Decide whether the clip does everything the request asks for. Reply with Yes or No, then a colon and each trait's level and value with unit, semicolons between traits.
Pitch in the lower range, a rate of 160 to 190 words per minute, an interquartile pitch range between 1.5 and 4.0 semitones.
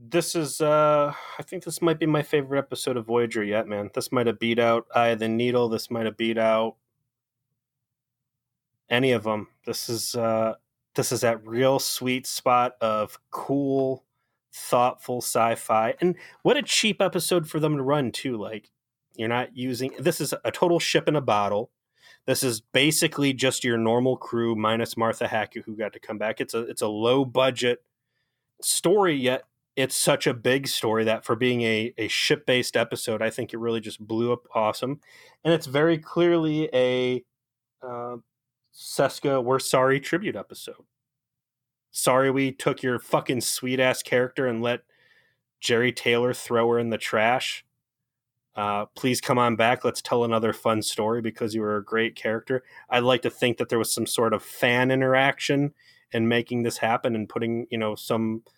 Yes: low, 125 Hz; average, 180 wpm; narrow, 2.6 semitones